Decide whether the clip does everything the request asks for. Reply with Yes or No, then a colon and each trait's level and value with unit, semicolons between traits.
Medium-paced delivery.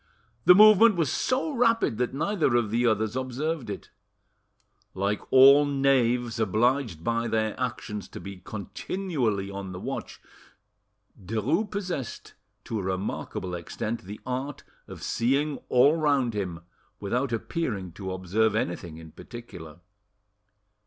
No: slow, 130 wpm